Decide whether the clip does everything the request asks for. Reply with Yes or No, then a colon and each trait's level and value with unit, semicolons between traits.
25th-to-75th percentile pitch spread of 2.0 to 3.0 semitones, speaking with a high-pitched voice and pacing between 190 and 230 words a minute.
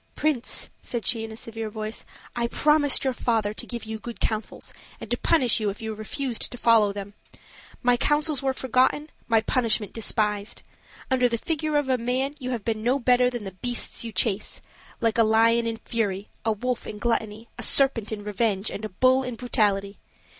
Yes: average, 2.7 semitones; high, 230 Hz; average, 195 wpm